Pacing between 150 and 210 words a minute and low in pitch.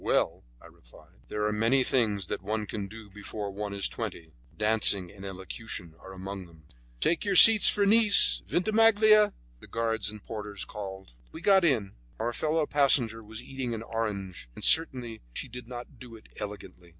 Yes: average, 175 wpm; low, 110 Hz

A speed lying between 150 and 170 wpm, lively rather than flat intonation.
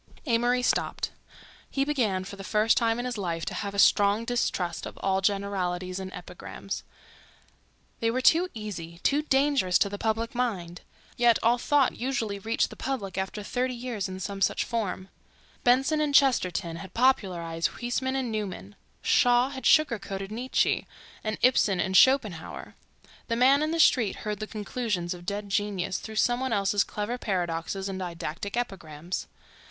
No: average, 165 wpm; average, 4.6 semitones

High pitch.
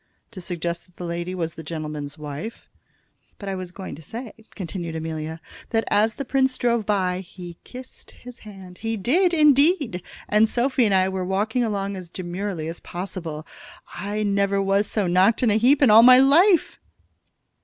Yes: high, 195 Hz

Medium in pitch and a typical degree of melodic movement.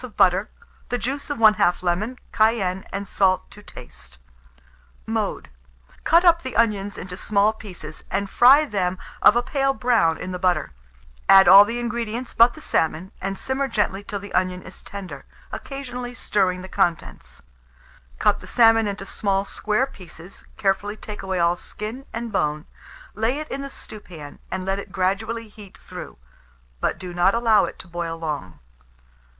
No: high, 200 Hz; average, 4.1 semitones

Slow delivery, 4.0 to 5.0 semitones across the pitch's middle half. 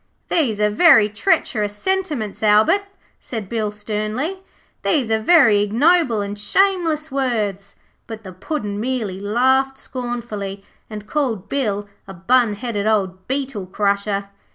Yes: slow, 130 wpm; average, 4.6 semitones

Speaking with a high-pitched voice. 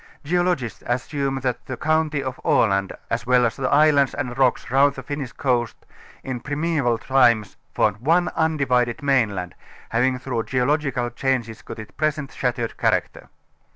No: low, 130 Hz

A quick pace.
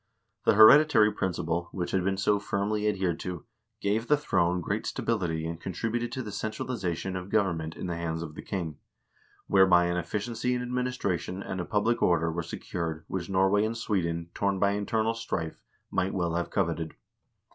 No: average, 175 wpm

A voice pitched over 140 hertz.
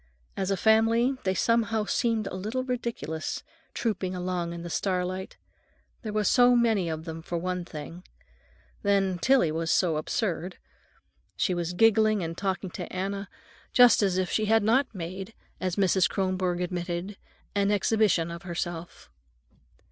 Yes: high, 190 Hz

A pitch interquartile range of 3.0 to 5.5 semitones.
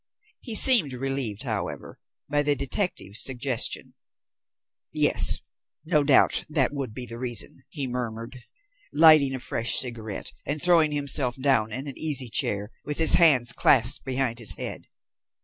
Yes: average, 3.6 semitones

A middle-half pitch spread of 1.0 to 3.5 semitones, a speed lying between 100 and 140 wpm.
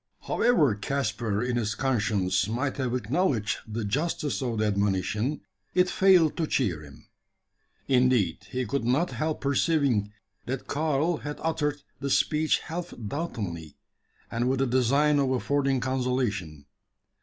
No: wide, 5.5 semitones; slow, 135 wpm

